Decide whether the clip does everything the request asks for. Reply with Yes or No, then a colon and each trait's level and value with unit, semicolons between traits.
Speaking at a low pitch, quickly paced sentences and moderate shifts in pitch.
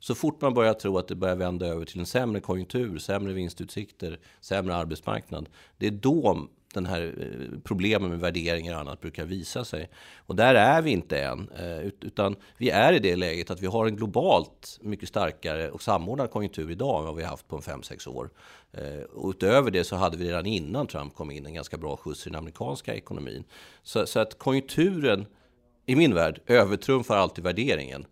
Yes: very low, 95 Hz; fast, 200 wpm; average, 3.8 semitones